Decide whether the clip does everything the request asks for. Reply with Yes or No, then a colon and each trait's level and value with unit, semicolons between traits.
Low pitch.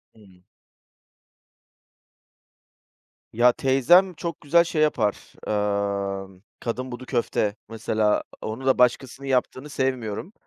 Yes: low, 125 Hz